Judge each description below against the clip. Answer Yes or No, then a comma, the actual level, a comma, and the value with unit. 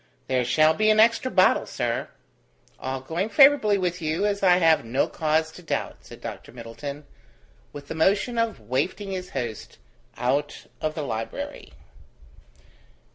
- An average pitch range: No, wide, 6.9 semitones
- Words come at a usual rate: Yes, average, 150 wpm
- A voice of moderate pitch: Yes, medium, 160 Hz